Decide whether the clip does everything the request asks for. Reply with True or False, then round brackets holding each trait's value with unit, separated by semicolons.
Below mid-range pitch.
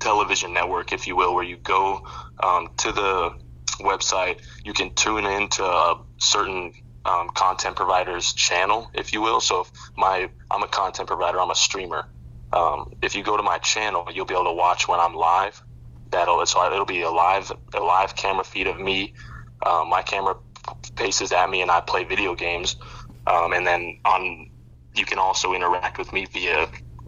True (85 Hz)